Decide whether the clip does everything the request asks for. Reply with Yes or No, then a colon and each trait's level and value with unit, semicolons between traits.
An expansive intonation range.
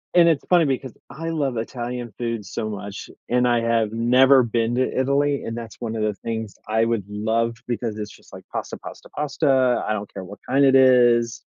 No: average, 2.9 semitones